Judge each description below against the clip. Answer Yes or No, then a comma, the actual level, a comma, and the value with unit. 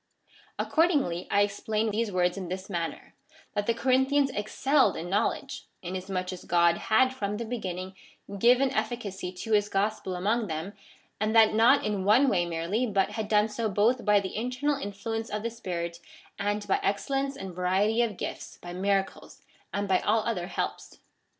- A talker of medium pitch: No, high, 205 Hz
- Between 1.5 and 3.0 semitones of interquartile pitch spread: No, average, 3.7 semitones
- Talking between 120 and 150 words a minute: No, average, 175 wpm